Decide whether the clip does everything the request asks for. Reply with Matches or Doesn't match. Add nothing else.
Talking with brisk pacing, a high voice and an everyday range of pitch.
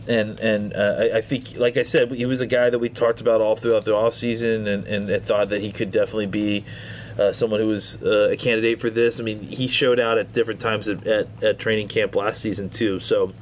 Doesn't match